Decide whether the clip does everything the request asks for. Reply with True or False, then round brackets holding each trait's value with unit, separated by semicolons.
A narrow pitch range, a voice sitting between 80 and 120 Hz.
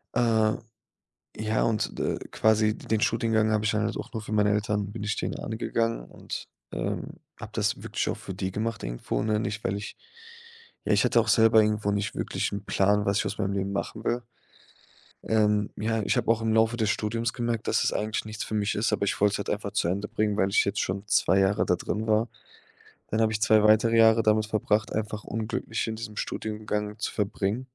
True (1.3 semitones; 110 Hz)